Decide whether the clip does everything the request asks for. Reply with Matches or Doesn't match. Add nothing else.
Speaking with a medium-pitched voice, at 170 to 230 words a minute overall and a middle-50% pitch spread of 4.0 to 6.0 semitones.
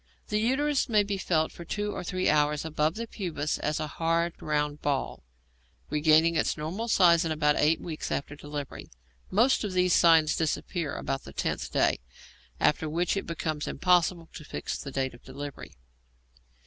Doesn't match